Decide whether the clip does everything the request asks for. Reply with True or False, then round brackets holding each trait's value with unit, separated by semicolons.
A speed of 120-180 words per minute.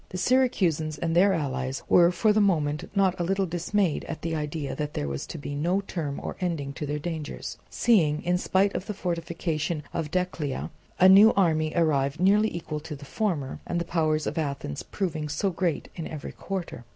False (200 wpm)